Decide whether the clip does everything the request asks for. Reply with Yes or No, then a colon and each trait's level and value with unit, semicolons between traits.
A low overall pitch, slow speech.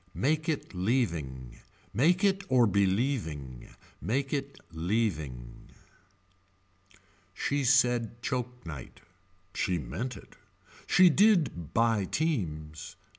Yes: low, 115 Hz; slow, 95 wpm